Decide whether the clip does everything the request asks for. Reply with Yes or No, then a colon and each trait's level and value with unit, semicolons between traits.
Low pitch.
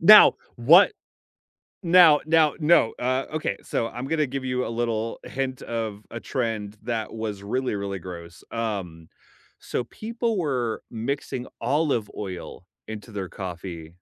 Yes: low, 115 Hz